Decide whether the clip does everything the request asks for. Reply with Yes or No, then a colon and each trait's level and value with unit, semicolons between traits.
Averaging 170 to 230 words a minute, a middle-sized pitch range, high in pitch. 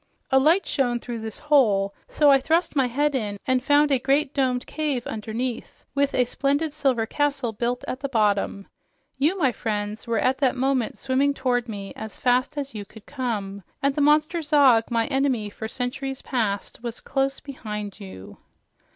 Yes: average, 180 wpm; average, 4.0 semitones; very high, 255 Hz